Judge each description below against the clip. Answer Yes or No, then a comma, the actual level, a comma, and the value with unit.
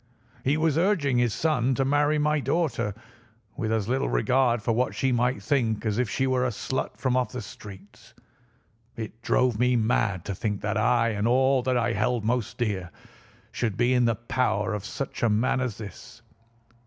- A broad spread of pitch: No, average, 3.2 semitones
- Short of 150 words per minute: No, average, 190 wpm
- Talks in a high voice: No, low, 120 Hz